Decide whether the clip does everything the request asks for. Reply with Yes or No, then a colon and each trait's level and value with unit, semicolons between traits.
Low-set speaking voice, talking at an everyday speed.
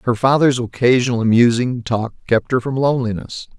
Yes: low, 120 Hz; average, 150 wpm